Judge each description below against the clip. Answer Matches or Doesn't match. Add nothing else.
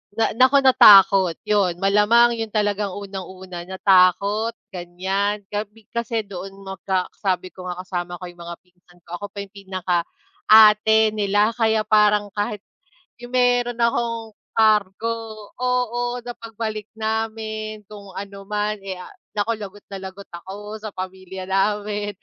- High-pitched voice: Matches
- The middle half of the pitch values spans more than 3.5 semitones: Doesn't match